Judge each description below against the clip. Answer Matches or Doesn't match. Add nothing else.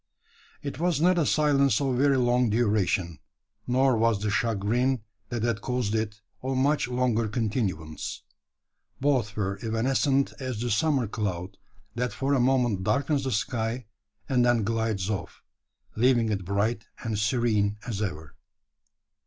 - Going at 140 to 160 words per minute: Matches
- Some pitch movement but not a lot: Matches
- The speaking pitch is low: Matches